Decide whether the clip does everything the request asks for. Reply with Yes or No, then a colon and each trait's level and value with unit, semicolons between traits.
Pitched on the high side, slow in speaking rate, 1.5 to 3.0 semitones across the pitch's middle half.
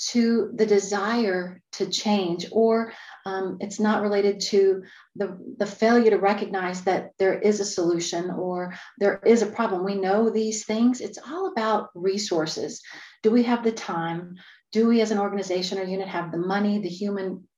No: high, 200 Hz; average, 175 wpm; average, 2.7 semitones